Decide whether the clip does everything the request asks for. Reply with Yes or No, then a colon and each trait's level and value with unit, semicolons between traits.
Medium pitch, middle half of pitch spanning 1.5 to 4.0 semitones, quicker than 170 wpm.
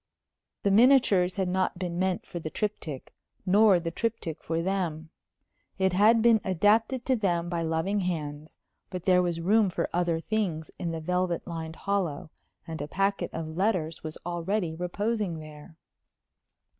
No: medium, 180 Hz; average, 3.6 semitones; average, 155 wpm